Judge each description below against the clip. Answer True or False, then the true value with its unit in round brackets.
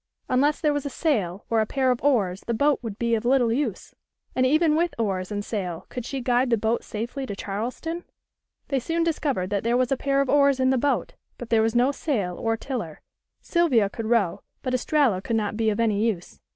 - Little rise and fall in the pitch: False (4.3 semitones)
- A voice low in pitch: False (240 Hz)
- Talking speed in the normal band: False (225 wpm)